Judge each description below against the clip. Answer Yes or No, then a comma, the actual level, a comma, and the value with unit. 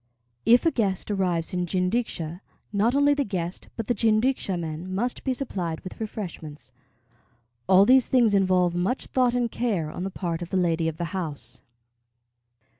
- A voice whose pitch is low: No, high, 190 Hz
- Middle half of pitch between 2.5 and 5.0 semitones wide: No, wide, 5.5 semitones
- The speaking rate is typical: Yes, average, 170 wpm